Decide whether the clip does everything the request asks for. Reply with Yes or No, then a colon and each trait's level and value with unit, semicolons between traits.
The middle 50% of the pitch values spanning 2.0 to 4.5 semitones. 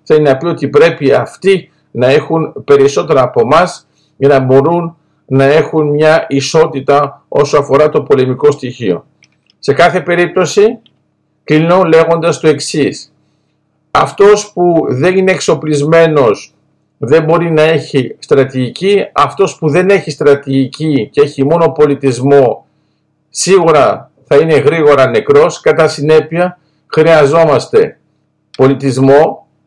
Yes: average, 3.2 semitones